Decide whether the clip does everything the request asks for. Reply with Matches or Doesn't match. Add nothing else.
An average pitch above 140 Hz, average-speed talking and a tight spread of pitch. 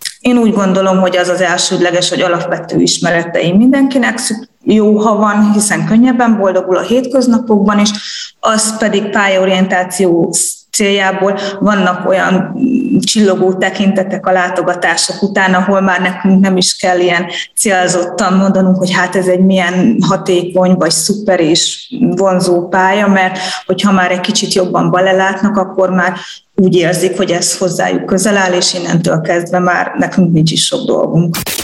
Matches